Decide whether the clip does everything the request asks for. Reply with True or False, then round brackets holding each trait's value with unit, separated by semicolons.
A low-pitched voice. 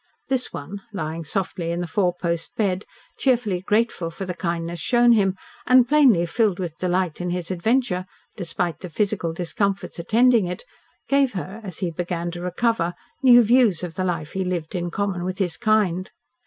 False (185 Hz)